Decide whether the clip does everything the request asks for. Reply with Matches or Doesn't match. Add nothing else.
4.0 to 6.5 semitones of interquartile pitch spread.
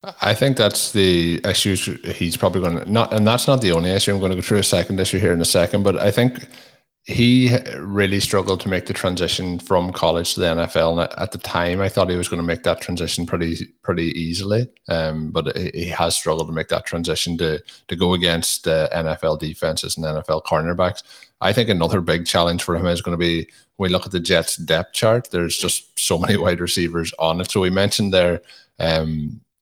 Doesn't match